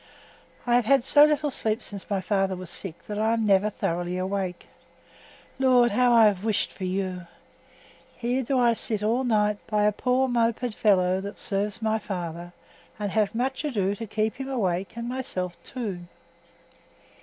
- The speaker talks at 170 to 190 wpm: Yes, average, 175 wpm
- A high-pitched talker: Yes, high, 215 Hz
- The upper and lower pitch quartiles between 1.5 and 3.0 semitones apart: No, average, 4.0 semitones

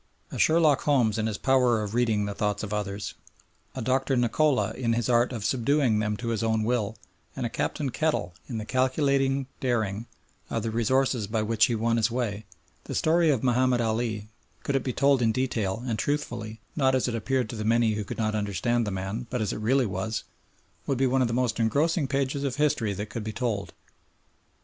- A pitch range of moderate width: Yes, average, 3.4 semitones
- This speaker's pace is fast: Yes, fast, 210 wpm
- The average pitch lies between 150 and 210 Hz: No, low, 115 Hz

